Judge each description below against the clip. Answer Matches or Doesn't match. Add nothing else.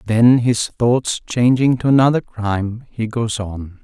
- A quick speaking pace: Doesn't match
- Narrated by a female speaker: Doesn't match